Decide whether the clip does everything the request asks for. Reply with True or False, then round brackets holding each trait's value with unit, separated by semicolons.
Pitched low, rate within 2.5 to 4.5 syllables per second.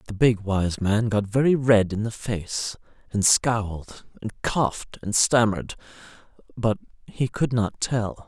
True (110 Hz; 4.0 syllables/s)